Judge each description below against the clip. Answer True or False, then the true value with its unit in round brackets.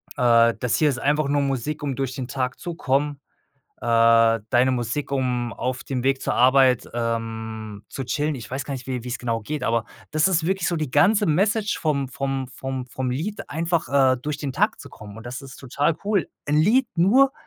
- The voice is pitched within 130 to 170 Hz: True (135 Hz)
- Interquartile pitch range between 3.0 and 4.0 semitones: True (3.7 semitones)